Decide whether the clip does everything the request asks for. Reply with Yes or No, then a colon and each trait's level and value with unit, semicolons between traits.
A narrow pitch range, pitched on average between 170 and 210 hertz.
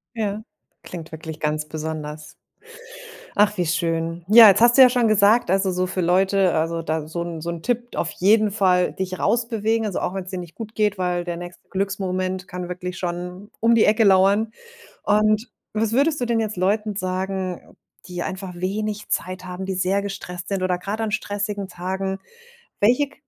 No: average, 3.0 semitones; high, 190 Hz